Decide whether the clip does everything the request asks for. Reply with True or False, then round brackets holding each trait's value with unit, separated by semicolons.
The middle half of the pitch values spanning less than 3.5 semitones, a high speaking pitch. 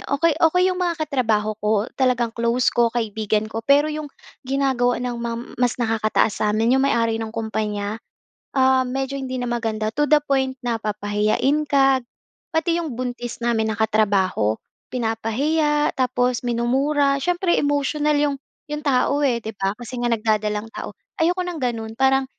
False (4.0 semitones; 245 Hz)